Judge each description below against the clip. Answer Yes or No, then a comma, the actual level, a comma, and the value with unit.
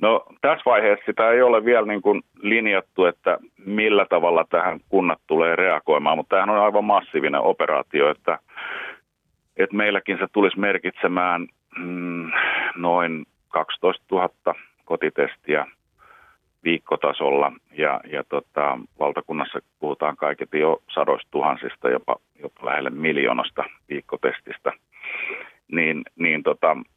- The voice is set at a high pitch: No, low, 105 Hz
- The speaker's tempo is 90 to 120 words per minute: Yes, average, 115 wpm